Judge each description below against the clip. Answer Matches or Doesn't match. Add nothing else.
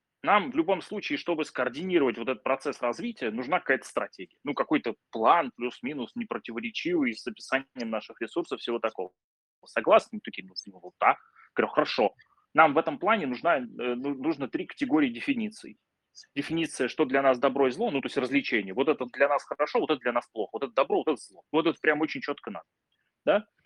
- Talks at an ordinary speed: Doesn't match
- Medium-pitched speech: Matches